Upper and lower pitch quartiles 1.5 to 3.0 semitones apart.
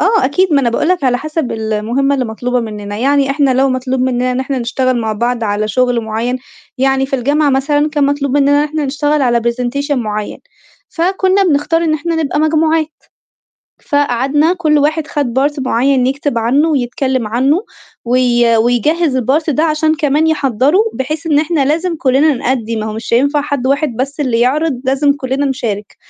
No: average, 3.6 semitones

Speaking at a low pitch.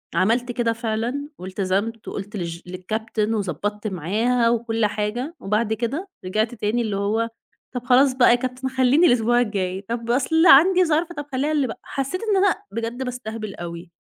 No: high, 230 Hz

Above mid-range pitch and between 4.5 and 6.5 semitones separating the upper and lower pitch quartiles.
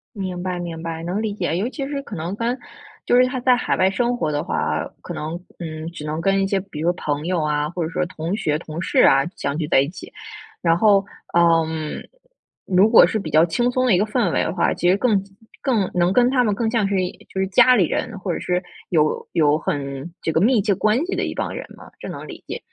No: medium, 180 Hz; average, 4.9 semitones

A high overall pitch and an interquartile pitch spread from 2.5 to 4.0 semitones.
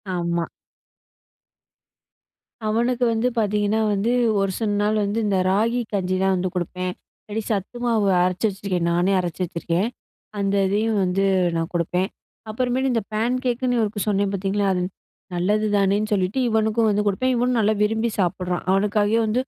Yes: high, 205 Hz; average, 3.1 semitones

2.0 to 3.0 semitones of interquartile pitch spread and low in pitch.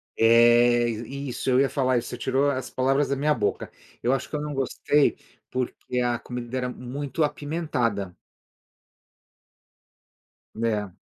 Yes: average, 2.7 semitones; low, 125 Hz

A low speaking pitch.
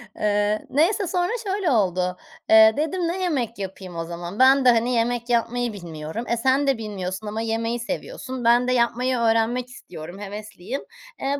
No: high, 230 Hz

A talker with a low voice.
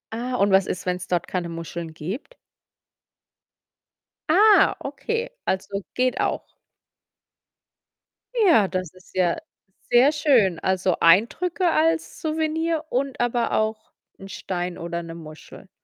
No: high, 205 Hz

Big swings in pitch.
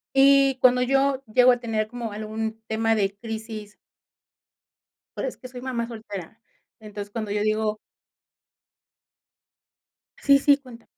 No: average, 2.9 semitones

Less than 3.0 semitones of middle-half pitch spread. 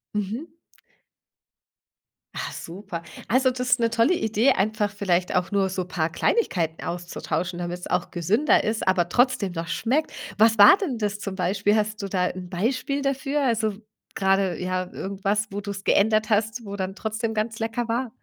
No: average, 3.7 semitones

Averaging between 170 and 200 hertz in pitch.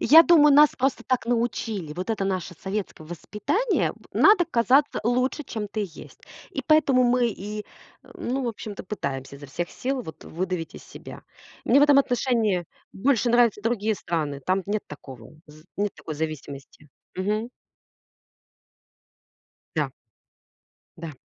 No: high, 210 Hz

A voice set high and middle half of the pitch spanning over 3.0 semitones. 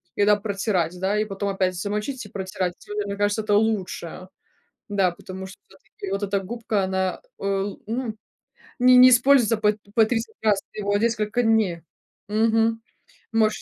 No: high, 205 Hz; narrow, 2.4 semitones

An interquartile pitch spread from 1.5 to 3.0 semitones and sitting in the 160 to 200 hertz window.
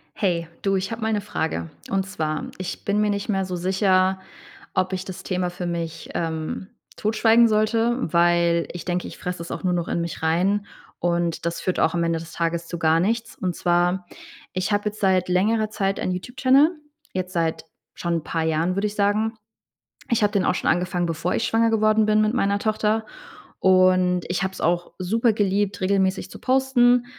No: average, 3.5 semitones; medium, 185 Hz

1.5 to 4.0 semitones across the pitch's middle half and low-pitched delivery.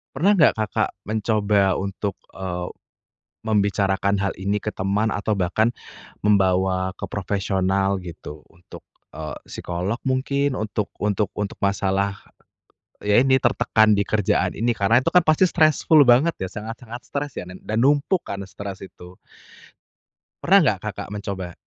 Yes: average, 3.3 semitones; low, 100 Hz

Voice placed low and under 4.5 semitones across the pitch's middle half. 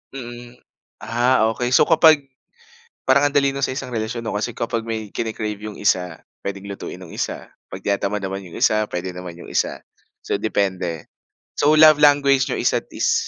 No: low, 110 Hz; average, 4.9 semitones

